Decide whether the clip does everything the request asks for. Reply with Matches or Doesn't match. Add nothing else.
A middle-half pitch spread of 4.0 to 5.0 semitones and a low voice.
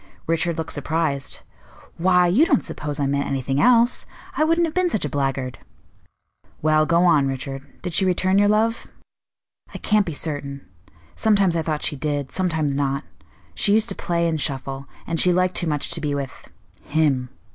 Doesn't match